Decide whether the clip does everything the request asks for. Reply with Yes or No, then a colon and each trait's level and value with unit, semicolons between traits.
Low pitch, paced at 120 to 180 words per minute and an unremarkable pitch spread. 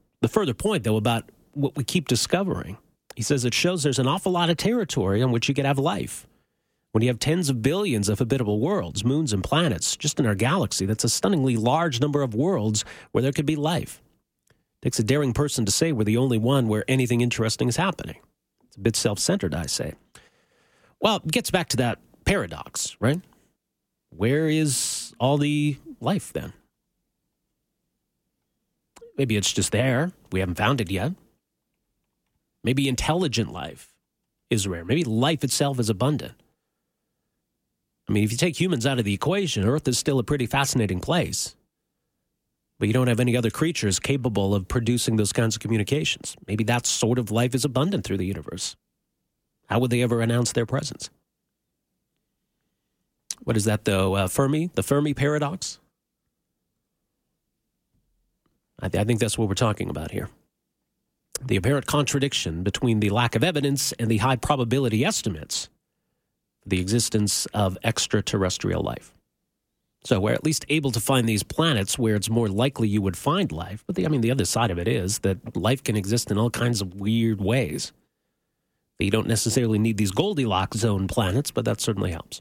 Yes: low, 120 Hz; average, 175 wpm; average, 4.7 semitones